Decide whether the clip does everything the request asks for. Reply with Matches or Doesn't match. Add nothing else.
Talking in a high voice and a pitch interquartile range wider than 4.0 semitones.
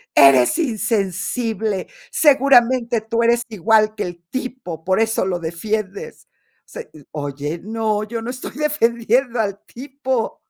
Matches